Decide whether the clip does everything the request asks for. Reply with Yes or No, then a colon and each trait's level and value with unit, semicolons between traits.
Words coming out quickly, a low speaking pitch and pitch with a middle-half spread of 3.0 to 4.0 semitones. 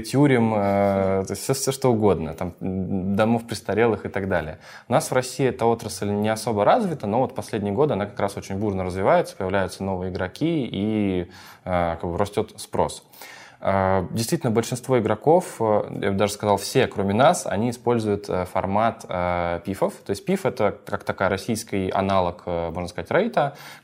Yes: fast, 165 wpm; low, 100 Hz; average, 3.4 semitones